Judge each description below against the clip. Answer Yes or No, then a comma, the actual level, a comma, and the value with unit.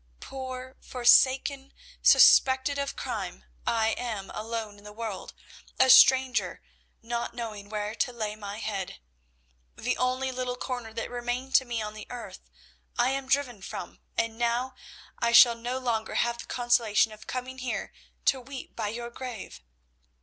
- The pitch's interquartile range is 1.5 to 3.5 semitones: Yes, average, 2.7 semitones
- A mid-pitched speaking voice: No, high, 240 Hz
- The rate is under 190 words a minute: Yes, average, 155 wpm